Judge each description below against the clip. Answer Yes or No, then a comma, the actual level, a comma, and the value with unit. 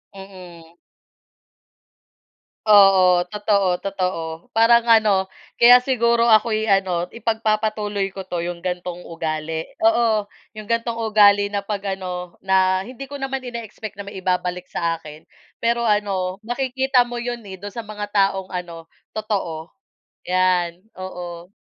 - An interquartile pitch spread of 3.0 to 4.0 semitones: Yes, average, 3.7 semitones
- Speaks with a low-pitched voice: No, high, 200 Hz